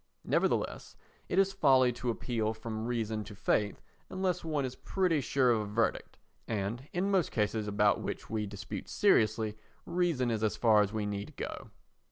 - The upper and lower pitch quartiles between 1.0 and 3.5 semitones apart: No, average, 5.2 semitones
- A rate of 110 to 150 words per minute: No, average, 175 wpm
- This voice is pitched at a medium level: No, low, 115 Hz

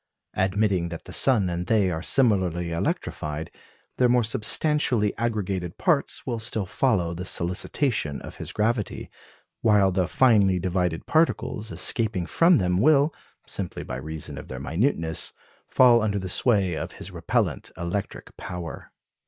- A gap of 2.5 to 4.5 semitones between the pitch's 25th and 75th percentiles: No, average, 5.0 semitones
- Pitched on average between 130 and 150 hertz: No, very low, 95 Hz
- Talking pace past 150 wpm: No, average, 145 wpm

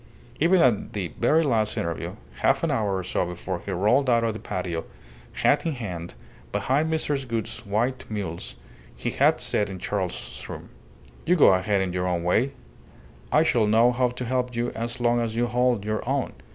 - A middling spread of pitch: Yes, average, 4.7 semitones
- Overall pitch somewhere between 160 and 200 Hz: No, low, 115 Hz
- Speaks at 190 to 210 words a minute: Yes, average, 195 wpm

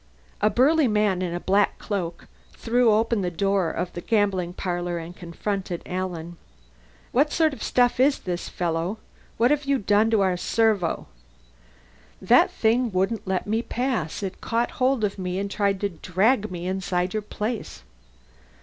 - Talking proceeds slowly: No, average, 165 wpm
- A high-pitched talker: Yes, high, 200 Hz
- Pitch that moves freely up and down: No, average, 4.1 semitones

